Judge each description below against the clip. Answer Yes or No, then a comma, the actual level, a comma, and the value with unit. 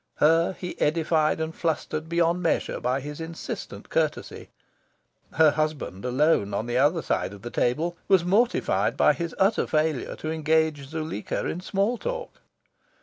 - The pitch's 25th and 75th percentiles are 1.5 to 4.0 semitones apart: Yes, narrow, 2.5 semitones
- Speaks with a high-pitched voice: No, medium, 160 Hz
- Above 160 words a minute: No, average, 150 wpm